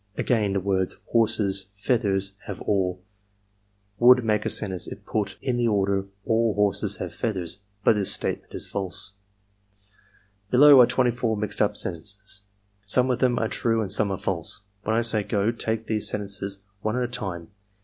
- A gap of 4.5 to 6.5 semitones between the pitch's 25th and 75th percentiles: No, average, 2.7 semitones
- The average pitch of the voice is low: Yes, low, 105 Hz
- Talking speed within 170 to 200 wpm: Yes, average, 180 wpm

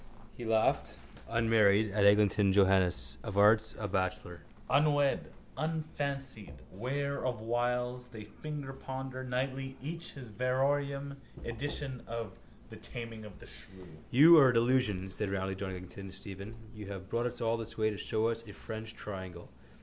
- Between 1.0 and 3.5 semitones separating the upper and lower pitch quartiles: No, average, 4.7 semitones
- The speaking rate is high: No, average, 155 wpm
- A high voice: No, low, 115 Hz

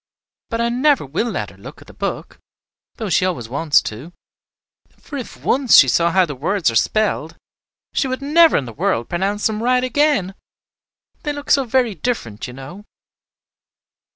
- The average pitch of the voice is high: Yes, high, 205 Hz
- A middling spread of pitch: No, wide, 8.9 semitones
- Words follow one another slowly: No, average, 180 wpm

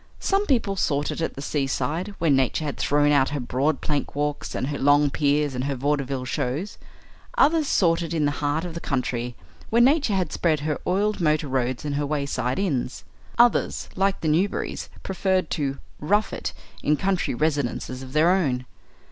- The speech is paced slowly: No, average, 185 wpm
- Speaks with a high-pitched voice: No, medium, 150 Hz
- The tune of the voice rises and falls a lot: No, average, 4.8 semitones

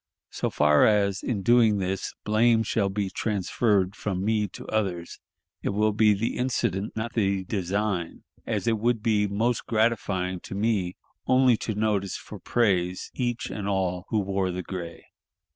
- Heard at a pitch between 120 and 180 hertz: No, low, 105 Hz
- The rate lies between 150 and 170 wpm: Yes, average, 160 wpm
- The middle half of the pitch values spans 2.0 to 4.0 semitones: Yes, average, 2.8 semitones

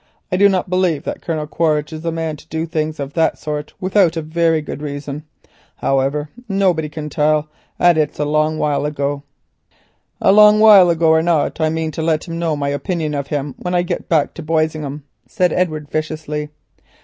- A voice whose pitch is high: No, medium, 155 Hz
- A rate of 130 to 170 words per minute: No, average, 200 wpm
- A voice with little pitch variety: Yes, narrow, 2.1 semitones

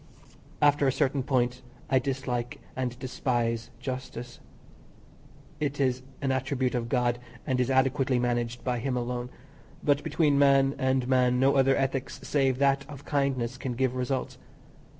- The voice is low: Yes, low, 130 Hz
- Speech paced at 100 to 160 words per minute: Yes, average, 150 wpm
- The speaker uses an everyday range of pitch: No, narrow, 1.7 semitones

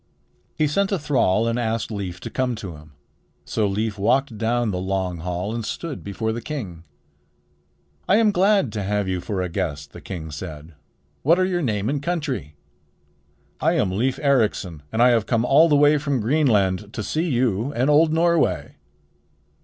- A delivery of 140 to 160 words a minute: No, average, 185 wpm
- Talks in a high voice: No, low, 115 Hz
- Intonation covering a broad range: Yes, wide, 7.3 semitones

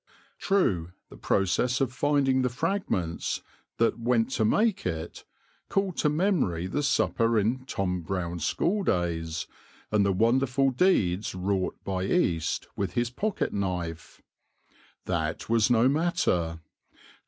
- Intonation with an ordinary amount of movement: No, wide, 7.1 semitones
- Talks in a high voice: No, low, 115 Hz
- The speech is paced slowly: Yes, slow, 130 wpm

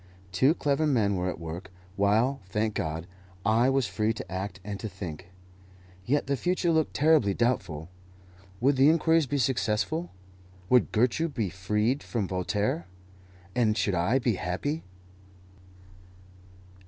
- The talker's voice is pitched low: Yes, low, 110 Hz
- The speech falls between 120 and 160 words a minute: Yes, average, 140 wpm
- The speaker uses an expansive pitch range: Yes, wide, 6.3 semitones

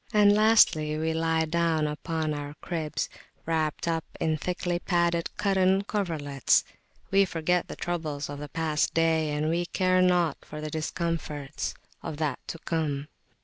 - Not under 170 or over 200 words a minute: No, average, 150 wpm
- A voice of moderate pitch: Yes, medium, 160 Hz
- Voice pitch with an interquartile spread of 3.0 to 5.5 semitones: No, narrow, 2.4 semitones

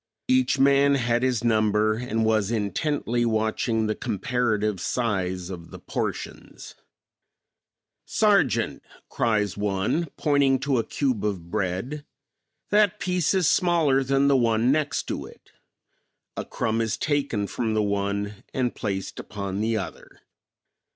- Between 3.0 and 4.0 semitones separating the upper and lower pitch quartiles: No, average, 4.7 semitones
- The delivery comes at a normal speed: No, slow, 130 wpm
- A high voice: No, low, 115 Hz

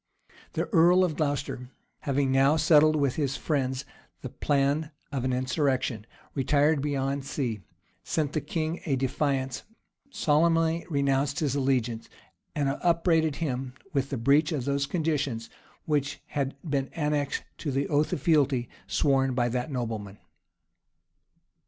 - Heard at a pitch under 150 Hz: Yes, medium, 140 Hz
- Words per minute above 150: No, slow, 135 wpm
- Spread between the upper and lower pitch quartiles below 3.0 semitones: Yes, narrow, 2.5 semitones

